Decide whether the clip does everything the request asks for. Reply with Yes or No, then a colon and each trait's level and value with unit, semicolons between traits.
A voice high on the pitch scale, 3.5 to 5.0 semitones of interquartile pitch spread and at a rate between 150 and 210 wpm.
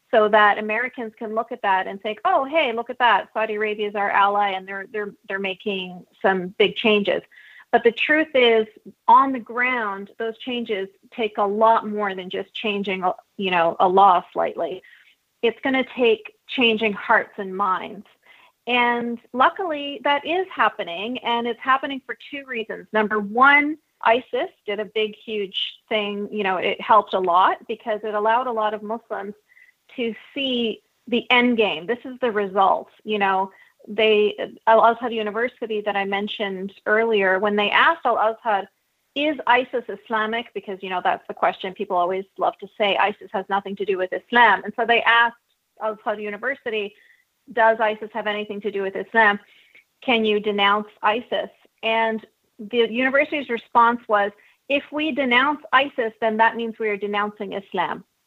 No: high, 220 Hz; average, 3.1 semitones; average, 175 wpm